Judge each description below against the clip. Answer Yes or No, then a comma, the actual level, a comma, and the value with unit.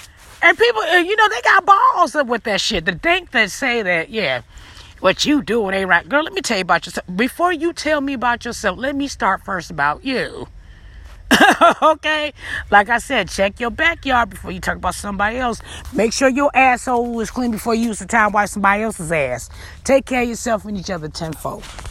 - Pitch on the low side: No, high, 235 Hz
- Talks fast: Yes, fast, 210 wpm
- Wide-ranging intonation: Yes, wide, 6.3 semitones